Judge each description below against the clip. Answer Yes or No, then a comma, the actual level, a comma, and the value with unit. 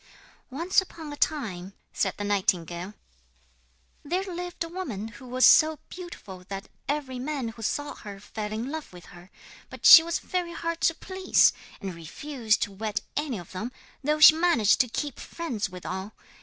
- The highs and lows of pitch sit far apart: Yes, wide, 7.7 semitones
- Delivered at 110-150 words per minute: No, average, 175 wpm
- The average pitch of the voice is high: Yes, very high, 255 Hz